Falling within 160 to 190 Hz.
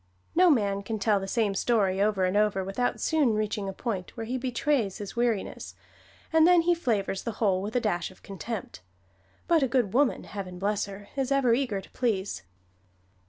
No: high, 215 Hz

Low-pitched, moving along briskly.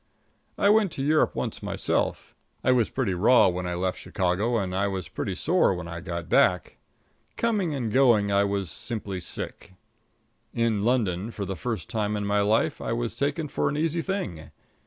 No: low, 105 Hz; average, 185 wpm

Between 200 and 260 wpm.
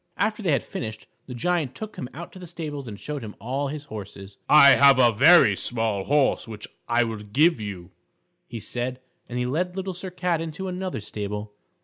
Yes: fast, 205 wpm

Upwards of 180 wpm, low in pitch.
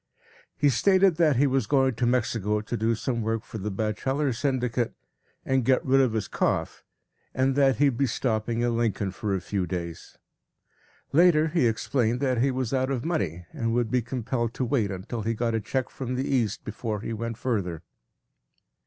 Yes: average, 195 wpm; low, 120 Hz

